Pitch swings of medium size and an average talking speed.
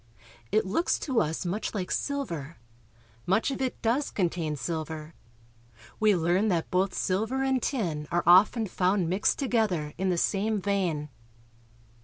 Yes: average, 4.6 semitones; average, 150 wpm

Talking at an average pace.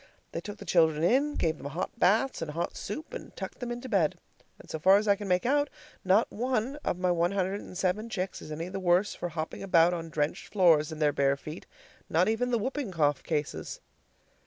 No: fast, 225 wpm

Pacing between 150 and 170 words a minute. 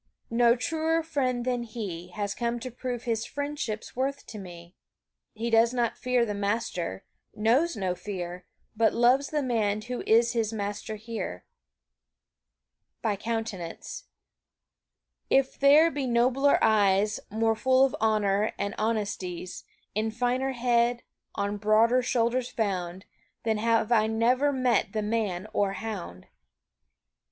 No: slow, 135 wpm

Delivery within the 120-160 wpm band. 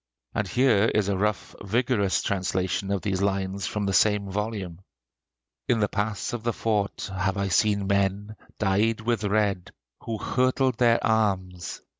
Yes: average, 155 wpm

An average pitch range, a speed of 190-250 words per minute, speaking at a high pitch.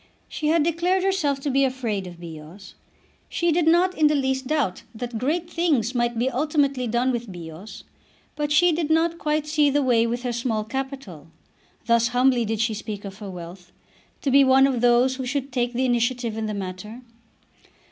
Yes: average, 4.9 semitones; average, 195 wpm; very high, 255 Hz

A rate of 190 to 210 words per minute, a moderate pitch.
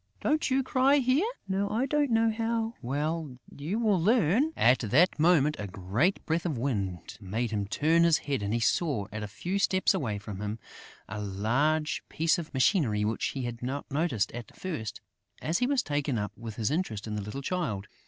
Yes: average, 200 wpm; medium, 145 Hz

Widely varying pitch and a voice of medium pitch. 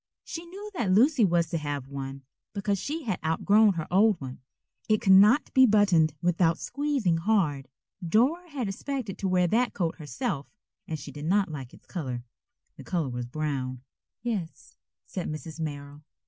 Yes: wide, 6.7 semitones; medium, 175 Hz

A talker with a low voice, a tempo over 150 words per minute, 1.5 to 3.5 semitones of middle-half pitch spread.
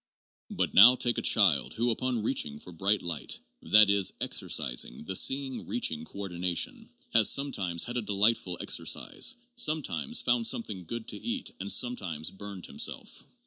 No: low, 105 Hz; average, 160 wpm; wide, 5.4 semitones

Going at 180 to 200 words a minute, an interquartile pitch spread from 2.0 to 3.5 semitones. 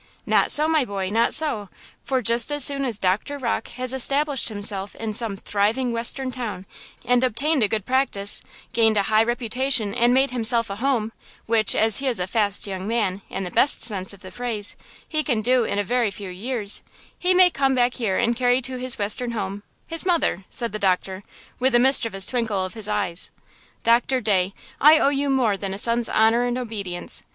No: average, 190 wpm; average, 4.0 semitones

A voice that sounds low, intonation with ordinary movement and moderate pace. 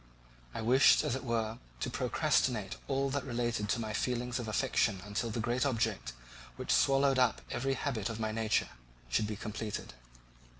Yes: low, 115 Hz; average, 3.0 semitones; average, 170 wpm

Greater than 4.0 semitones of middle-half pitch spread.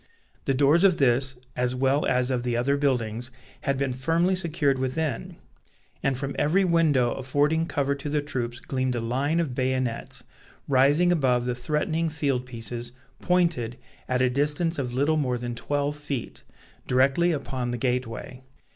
No: average, 3.1 semitones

